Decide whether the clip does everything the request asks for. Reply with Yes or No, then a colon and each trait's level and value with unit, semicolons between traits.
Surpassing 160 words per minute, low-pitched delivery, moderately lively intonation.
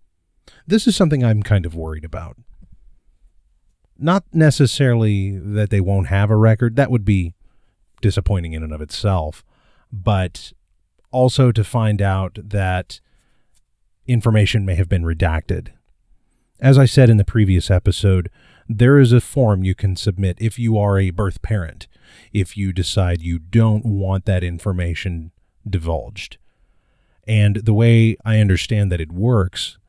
No: average, 145 wpm; low, 100 Hz; average, 3.6 semitones